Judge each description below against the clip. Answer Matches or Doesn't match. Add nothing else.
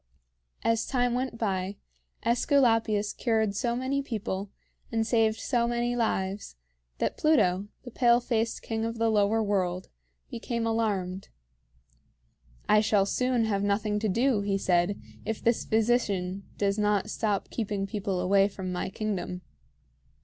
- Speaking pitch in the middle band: Doesn't match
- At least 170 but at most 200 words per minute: Doesn't match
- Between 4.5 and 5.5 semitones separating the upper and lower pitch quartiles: Doesn't match